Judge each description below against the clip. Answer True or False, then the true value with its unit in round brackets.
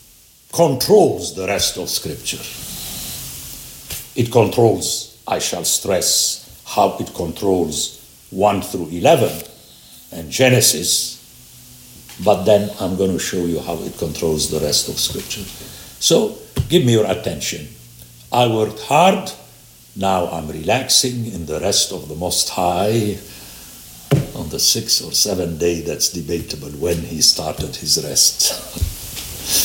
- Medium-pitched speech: False (95 Hz)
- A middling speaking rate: False (125 wpm)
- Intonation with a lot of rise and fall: True (6.8 semitones)